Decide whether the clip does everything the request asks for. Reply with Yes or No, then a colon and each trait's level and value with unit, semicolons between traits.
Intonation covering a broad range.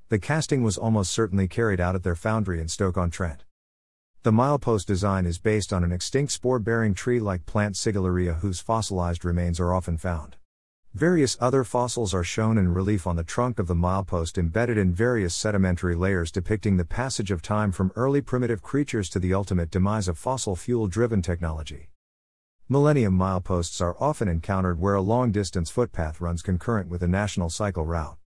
No: average, 4.3 semitones